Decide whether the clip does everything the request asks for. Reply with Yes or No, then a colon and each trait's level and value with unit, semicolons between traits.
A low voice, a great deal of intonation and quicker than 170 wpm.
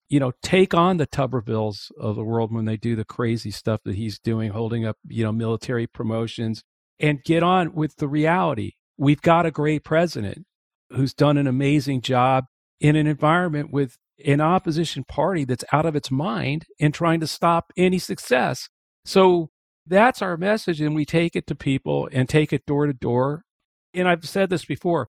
No: medium, 145 Hz; wide, 5.8 semitones; average, 190 wpm